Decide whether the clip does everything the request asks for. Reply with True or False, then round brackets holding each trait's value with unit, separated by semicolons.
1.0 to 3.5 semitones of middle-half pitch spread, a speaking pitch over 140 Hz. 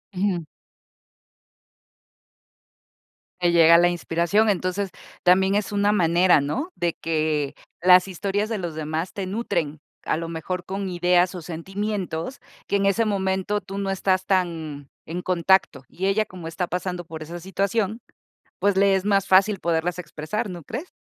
True (2.9 semitones; 185 Hz)